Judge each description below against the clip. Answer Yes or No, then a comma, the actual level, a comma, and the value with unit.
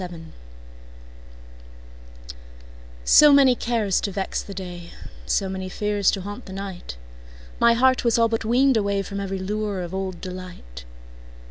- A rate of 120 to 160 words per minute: Yes, slow, 135 wpm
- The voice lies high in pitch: Yes, high, 195 Hz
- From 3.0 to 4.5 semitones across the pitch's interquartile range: Yes, average, 3.3 semitones